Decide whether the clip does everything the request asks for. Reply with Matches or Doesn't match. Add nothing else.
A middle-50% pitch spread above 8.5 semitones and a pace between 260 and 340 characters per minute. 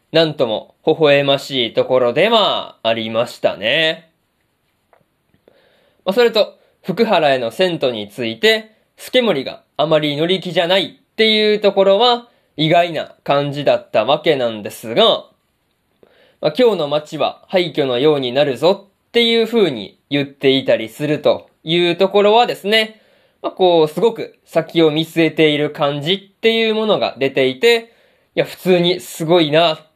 Doesn't match